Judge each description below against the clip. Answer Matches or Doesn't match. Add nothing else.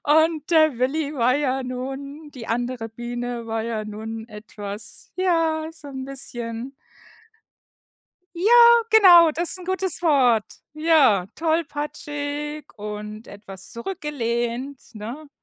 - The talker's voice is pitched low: Doesn't match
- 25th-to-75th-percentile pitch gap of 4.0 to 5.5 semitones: Matches